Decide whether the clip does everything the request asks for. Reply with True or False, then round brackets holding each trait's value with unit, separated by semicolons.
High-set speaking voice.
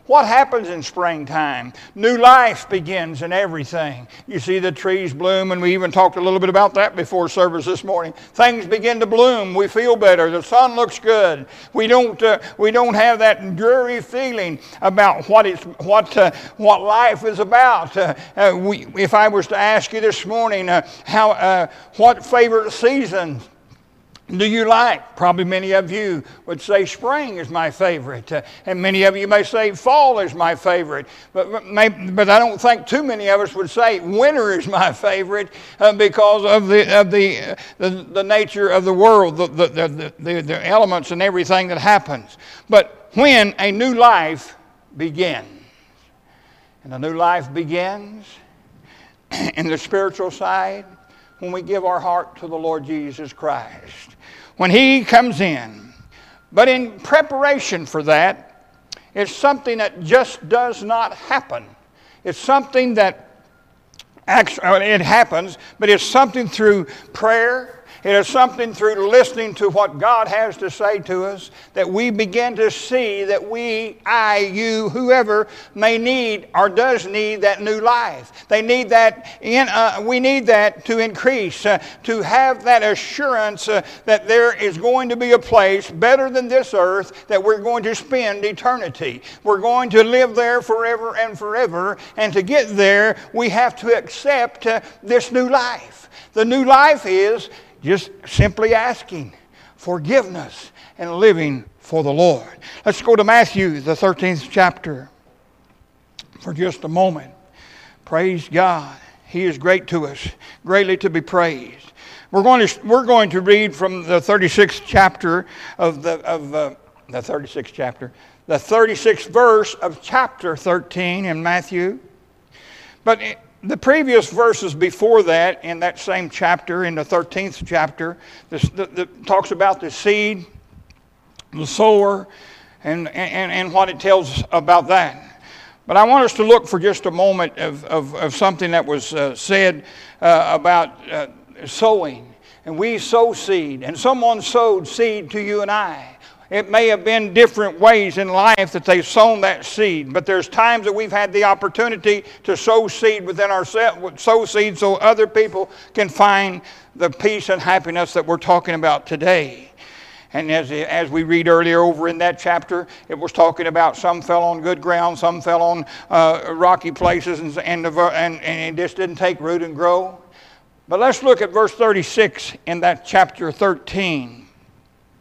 True (200 Hz)